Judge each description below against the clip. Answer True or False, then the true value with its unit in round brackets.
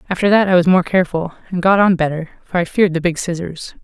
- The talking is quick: True (250 wpm)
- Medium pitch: True (175 Hz)